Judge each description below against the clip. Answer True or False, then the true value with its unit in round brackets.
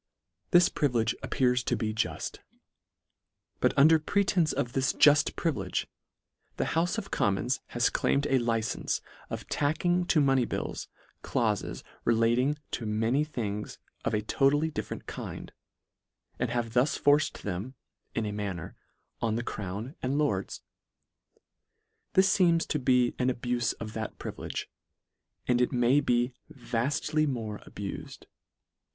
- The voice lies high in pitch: False (125 Hz)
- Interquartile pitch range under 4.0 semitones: False (4.5 semitones)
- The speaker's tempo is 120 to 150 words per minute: True (140 wpm)